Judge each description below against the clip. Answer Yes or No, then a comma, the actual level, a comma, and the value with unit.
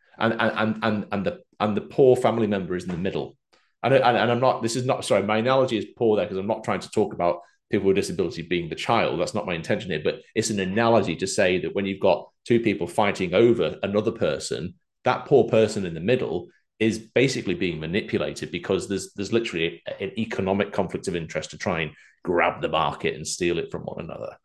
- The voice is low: Yes, low, 105 Hz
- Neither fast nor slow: No, fast, 230 wpm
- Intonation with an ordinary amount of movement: Yes, average, 3.0 semitones